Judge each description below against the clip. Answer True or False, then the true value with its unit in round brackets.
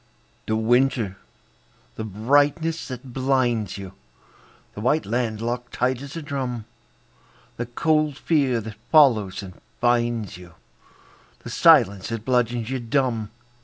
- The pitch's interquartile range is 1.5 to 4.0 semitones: True (3.6 semitones)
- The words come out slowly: True (130 wpm)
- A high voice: False (120 Hz)